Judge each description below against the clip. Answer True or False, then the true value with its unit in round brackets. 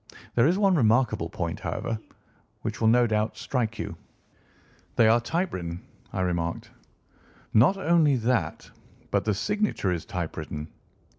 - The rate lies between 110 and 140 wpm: True (135 wpm)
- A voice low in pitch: True (110 Hz)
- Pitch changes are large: True (7.0 semitones)